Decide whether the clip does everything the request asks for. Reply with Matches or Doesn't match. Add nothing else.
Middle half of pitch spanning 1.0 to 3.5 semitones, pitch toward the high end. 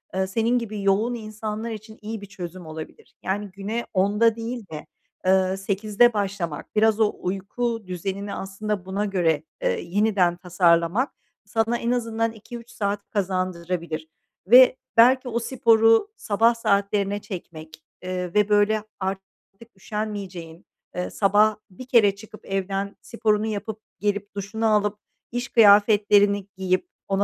Matches